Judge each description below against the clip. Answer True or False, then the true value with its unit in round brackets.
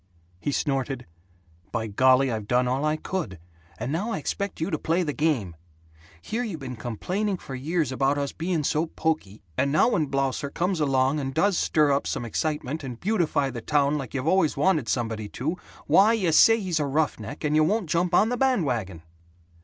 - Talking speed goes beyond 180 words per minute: True (195 wpm)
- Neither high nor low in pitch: True (150 Hz)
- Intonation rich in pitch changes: False (4.7 semitones)